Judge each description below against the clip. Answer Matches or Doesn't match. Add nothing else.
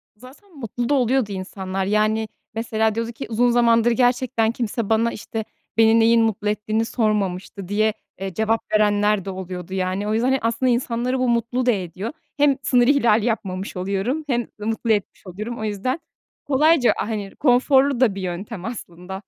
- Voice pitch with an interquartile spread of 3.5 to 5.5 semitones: Doesn't match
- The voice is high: Matches